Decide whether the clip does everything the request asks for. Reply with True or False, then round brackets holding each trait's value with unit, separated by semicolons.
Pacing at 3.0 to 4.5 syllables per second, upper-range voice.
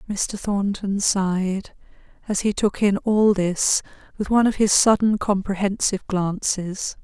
True (4.2 syllables/s; 200 Hz)